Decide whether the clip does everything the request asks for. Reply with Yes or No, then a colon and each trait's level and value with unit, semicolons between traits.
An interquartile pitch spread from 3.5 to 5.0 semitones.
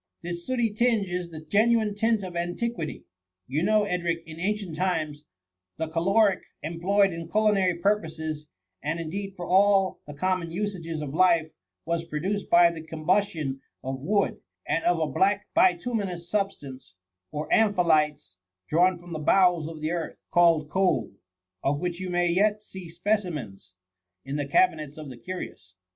Yes: average, 3.9 semitones